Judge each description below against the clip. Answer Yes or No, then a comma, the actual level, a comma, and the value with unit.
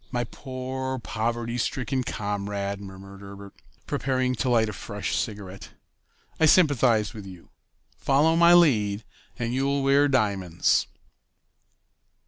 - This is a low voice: Yes, low, 115 Hz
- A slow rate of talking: Yes, slow, 115 wpm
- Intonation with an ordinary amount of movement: Yes, average, 4.7 semitones